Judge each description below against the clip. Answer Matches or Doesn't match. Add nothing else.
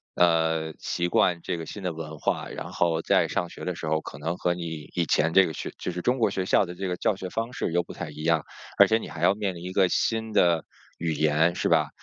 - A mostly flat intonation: Matches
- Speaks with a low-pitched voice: Matches